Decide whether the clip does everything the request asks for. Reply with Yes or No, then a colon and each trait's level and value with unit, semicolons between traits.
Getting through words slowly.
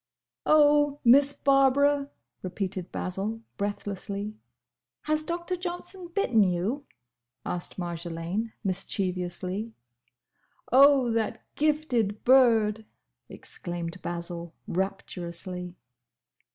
Yes: slow, 75 wpm